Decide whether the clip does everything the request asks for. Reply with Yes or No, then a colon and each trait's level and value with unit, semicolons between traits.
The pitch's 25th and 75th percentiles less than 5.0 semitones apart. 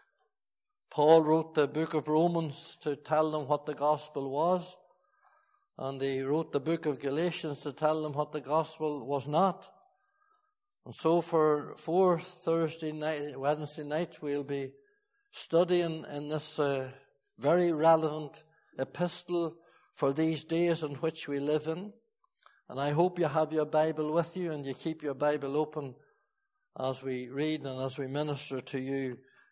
Yes: average, 2.8 semitones